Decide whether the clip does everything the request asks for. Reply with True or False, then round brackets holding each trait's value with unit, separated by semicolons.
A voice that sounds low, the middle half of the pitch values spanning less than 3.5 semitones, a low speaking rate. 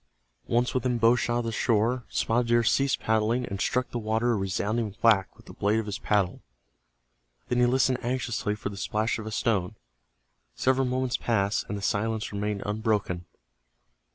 False (110 Hz; 2.6 semitones; 180 wpm)